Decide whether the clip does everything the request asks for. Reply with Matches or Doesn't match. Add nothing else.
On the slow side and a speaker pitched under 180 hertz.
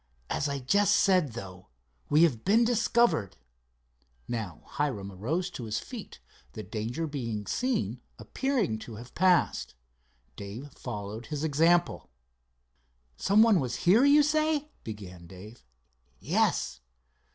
Matches